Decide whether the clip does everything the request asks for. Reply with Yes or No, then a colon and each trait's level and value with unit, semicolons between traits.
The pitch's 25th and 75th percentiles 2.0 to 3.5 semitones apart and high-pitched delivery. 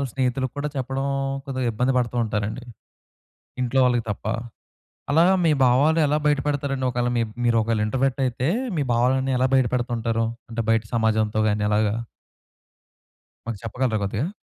No: average, 2.8 semitones; low, 125 Hz